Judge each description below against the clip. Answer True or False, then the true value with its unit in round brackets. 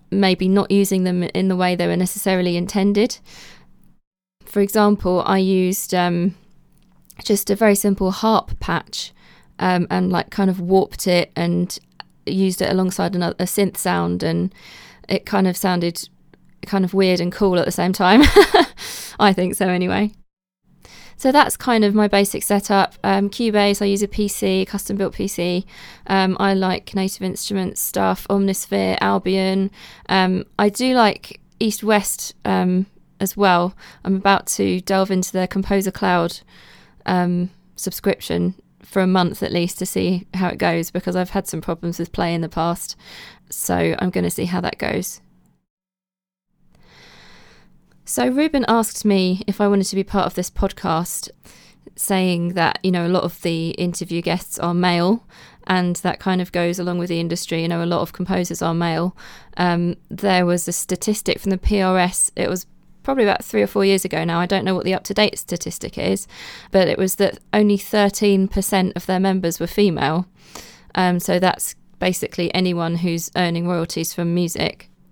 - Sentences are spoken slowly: False (175 wpm)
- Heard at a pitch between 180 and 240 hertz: True (185 Hz)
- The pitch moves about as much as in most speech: False (2.0 semitones)